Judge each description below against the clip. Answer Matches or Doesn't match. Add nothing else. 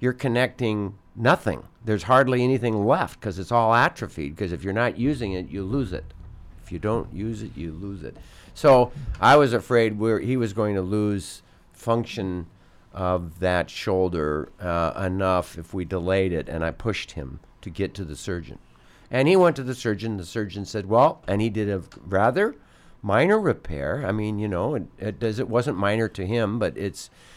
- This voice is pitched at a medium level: Doesn't match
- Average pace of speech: Matches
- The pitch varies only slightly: Doesn't match